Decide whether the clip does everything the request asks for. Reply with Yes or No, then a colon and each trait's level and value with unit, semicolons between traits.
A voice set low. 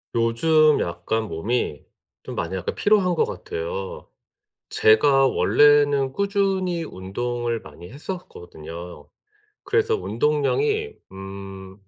Yes: low, 120 Hz